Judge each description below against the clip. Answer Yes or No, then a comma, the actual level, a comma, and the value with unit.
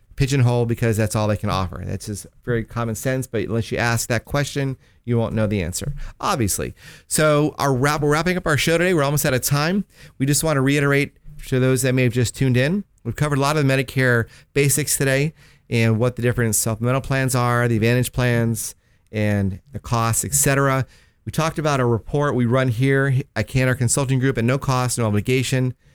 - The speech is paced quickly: Yes, fast, 210 wpm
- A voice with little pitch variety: No, average, 3.5 semitones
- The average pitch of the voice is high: No, low, 130 Hz